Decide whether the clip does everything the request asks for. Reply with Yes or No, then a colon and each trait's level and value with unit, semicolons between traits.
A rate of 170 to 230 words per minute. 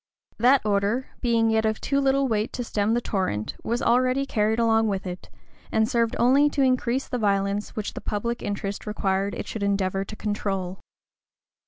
Yes: average, 185 wpm